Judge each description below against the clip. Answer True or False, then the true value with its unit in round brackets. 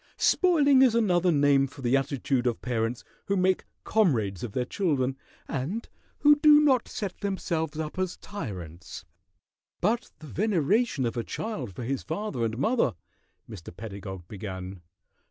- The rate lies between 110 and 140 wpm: False (155 wpm)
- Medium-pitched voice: True (145 Hz)